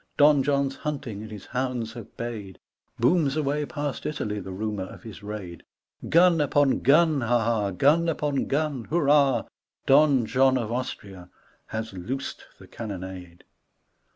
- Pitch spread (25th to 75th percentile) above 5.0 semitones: Yes, wide, 5.5 semitones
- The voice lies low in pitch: Yes, low, 125 Hz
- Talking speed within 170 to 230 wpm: No, average, 155 wpm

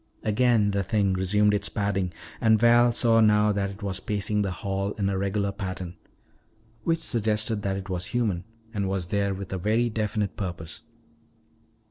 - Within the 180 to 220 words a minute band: No, average, 170 wpm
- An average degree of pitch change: No, narrow, 1.9 semitones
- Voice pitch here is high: No, low, 100 Hz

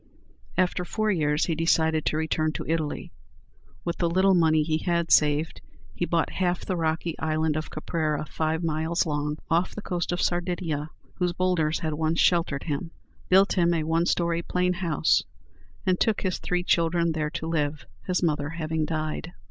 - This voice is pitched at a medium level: Yes, medium, 165 Hz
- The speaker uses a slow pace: No, average, 175 wpm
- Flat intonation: Yes, narrow, 2.1 semitones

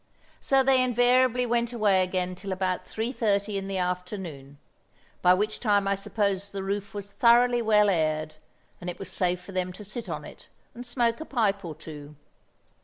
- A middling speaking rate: Yes, average, 180 wpm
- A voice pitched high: Yes, high, 200 Hz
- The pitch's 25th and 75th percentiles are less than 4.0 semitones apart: No, average, 4.3 semitones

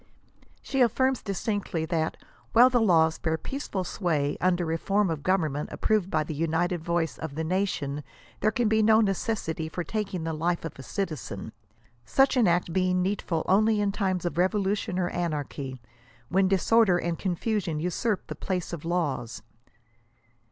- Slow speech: No, average, 170 wpm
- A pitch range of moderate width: Yes, average, 4.1 semitones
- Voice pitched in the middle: Yes, medium, 180 Hz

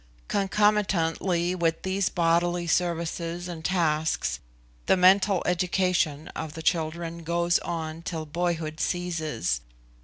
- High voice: No, medium, 170 Hz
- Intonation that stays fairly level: Yes, narrow, 1.8 semitones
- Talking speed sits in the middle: No, slow, 110 wpm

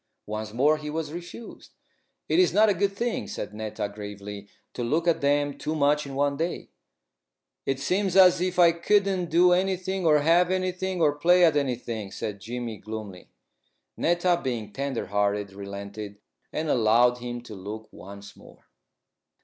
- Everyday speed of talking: Yes, average, 165 wpm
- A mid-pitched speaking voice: Yes, medium, 145 Hz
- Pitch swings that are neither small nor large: No, wide, 8.5 semitones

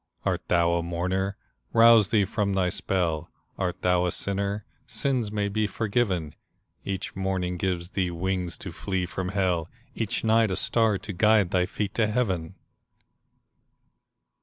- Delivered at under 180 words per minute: Yes, average, 150 wpm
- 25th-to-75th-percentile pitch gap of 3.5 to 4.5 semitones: No, average, 2.8 semitones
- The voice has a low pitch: Yes, very low, 95 Hz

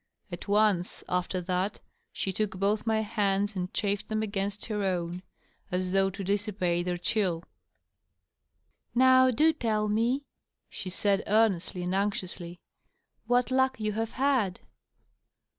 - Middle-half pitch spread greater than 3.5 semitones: No, average, 3.0 semitones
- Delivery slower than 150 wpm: Yes, average, 140 wpm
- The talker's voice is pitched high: Yes, high, 205 Hz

